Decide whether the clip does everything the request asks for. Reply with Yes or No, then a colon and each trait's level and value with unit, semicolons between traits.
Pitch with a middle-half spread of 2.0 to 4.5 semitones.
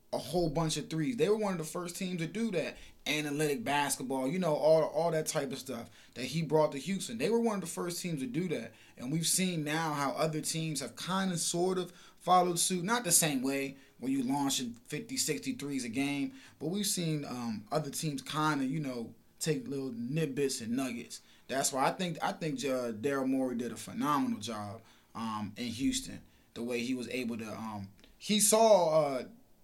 No: average, 5.0 semitones